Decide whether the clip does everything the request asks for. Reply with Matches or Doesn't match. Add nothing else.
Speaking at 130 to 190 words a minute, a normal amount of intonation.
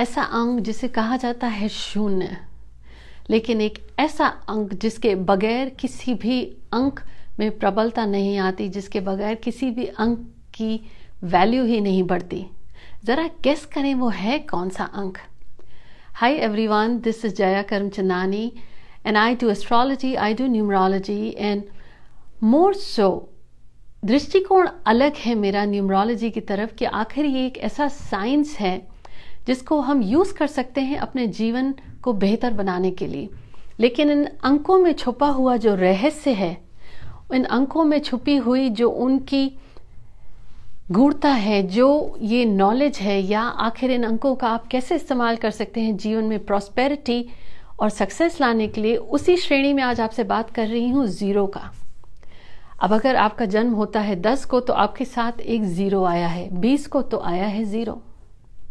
Matches